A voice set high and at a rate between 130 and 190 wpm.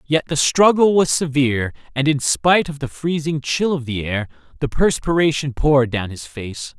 No: medium, 140 Hz; average, 185 wpm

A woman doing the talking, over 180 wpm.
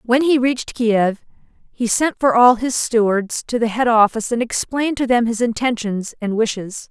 Yes: female; average, 190 wpm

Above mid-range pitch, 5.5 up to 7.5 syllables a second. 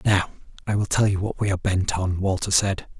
No: low, 100 Hz; 5.7 syllables/s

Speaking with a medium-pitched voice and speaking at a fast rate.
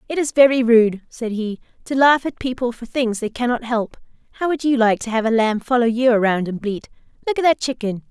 No: high, 240 Hz; fast, 235 wpm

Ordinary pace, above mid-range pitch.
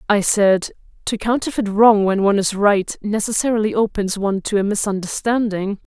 Yes: average, 150 wpm; high, 205 Hz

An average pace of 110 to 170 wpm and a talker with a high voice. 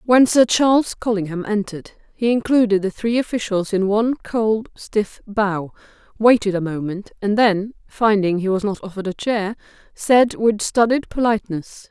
Yes: average, 155 wpm; high, 215 Hz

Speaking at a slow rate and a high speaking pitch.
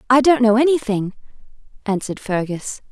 Yes: slow, 125 wpm; high, 230 Hz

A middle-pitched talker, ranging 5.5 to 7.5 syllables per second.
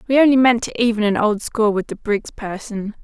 No: high, 220 Hz; 5.6 syllables/s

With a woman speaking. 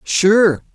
No: male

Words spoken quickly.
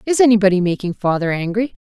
No: average, 165 wpm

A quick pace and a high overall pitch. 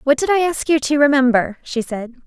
Yes: fast, 240 wpm; very high, 270 Hz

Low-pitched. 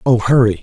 Yes: low, 115 Hz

